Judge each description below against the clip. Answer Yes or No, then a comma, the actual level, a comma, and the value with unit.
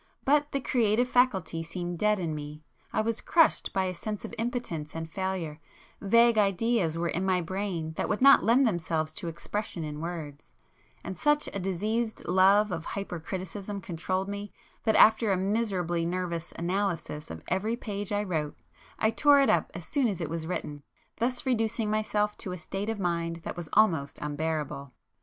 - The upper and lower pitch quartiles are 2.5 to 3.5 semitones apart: No, average, 4.6 semitones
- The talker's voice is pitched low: No, high, 190 Hz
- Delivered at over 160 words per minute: Yes, average, 175 wpm